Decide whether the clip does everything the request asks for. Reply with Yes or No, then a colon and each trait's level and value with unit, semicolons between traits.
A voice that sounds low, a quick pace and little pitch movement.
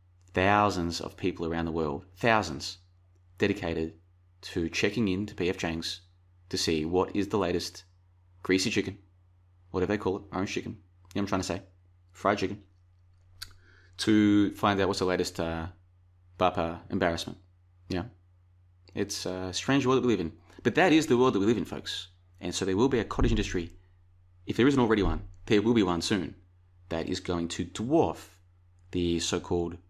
No: very low, 90 Hz; average, 180 wpm; narrow, 1.2 semitones